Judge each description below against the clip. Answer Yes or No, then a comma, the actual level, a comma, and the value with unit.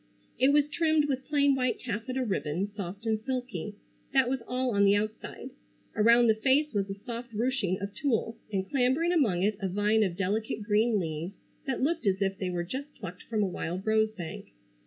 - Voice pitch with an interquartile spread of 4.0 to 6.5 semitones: Yes, average, 4.7 semitones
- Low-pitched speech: No, high, 220 Hz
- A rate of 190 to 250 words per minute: Yes, average, 200 wpm